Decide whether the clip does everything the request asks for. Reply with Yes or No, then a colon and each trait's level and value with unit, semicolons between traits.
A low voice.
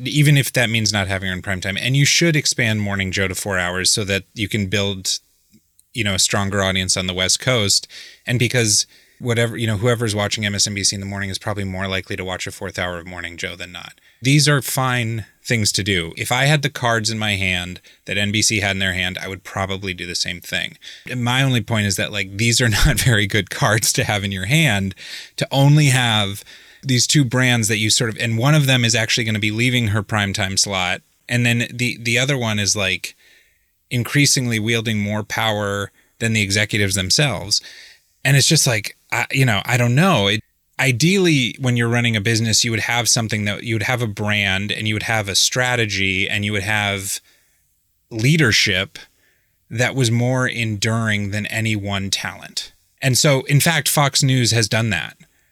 Yes: low, 110 Hz